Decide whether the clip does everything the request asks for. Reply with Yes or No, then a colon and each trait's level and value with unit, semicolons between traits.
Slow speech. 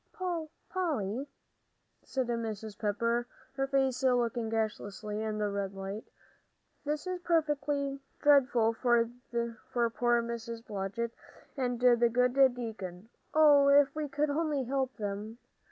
Yes: slow, 120 wpm